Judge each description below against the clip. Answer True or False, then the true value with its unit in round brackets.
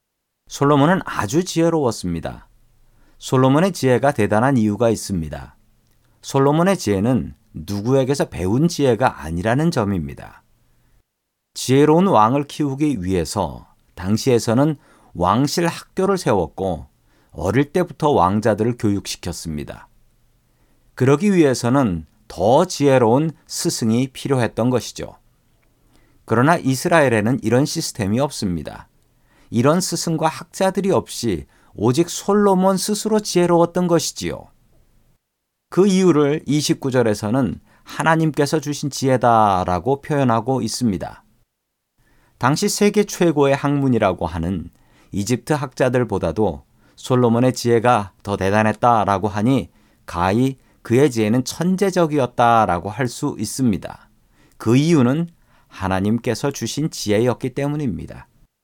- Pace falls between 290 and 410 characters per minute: False (280 characters per minute)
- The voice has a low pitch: True (125 Hz)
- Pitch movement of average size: False (6.0 semitones)